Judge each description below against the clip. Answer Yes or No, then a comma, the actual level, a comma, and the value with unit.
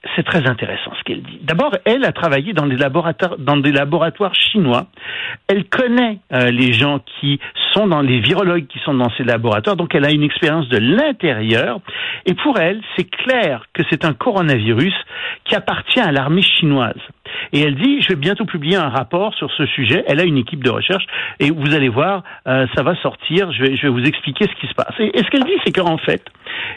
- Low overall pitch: No, medium, 160 Hz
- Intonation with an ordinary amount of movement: No, wide, 5.8 semitones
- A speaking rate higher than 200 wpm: Yes, average, 215 wpm